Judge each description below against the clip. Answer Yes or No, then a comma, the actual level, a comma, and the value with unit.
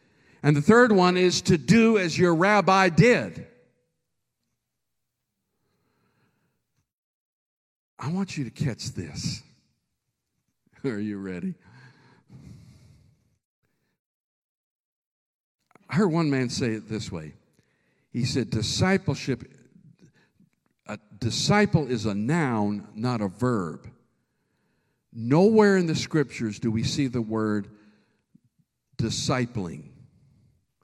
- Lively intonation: Yes, wide, 8.3 semitones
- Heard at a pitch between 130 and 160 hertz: Yes, low, 135 Hz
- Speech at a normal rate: No, slow, 95 wpm